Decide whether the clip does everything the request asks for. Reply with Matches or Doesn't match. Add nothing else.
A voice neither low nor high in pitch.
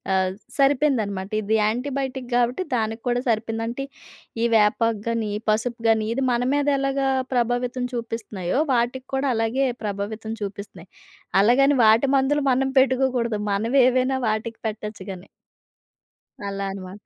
Doesn't match